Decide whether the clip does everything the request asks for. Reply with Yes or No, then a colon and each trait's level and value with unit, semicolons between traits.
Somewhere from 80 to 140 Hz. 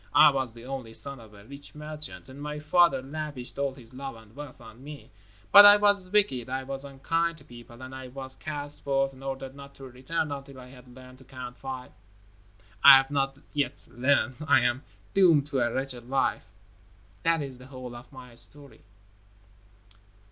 Yes: low, 135 Hz